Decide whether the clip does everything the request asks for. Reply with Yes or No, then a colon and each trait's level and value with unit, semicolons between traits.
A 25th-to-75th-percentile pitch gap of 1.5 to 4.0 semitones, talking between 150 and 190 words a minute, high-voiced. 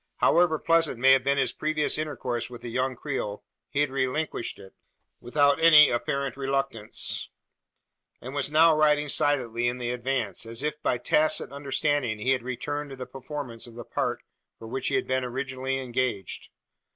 No: average, 3.2 semitones; average, 175 wpm; low, 135 Hz